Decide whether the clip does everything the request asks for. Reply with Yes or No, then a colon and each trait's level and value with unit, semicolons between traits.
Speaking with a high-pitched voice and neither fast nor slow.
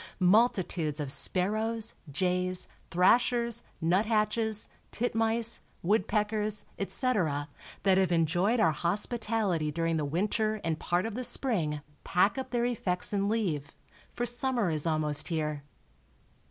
No: high, 195 Hz; slow, 120 wpm